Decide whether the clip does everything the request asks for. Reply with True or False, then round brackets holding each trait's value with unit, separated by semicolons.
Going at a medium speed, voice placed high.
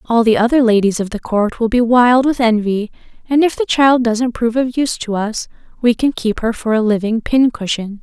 False (225 wpm; 235 Hz)